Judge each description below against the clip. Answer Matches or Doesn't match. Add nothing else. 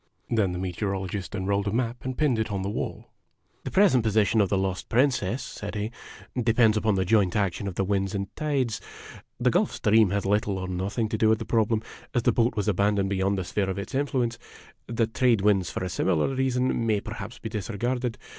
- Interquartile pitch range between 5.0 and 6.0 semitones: Doesn't match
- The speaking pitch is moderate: Doesn't match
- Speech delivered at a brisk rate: Matches